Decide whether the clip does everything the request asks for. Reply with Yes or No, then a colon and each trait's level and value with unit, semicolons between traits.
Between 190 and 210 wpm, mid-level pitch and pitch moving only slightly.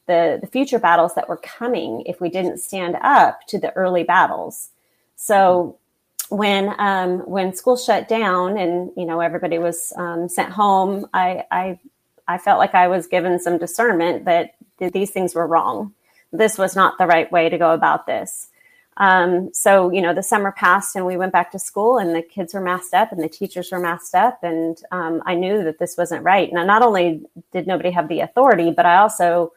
Yes: fast, 205 wpm; medium, 180 Hz; narrow, 2.3 semitones